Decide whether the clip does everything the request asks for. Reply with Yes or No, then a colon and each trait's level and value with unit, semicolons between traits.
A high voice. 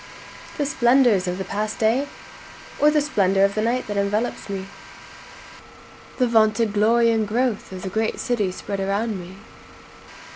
Yes: high, 215 Hz